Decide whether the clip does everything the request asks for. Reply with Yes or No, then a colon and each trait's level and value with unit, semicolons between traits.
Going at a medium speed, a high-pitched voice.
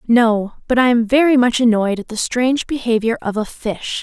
No: fast, 210 wpm; high, 235 Hz